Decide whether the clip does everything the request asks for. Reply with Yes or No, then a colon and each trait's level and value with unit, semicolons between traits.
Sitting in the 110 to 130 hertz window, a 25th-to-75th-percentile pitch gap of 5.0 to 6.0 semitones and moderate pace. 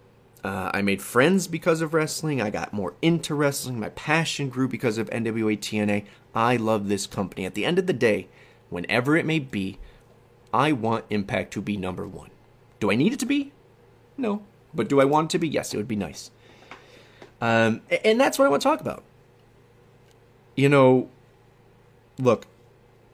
Yes: low, 120 Hz; wide, 5.6 semitones; average, 185 wpm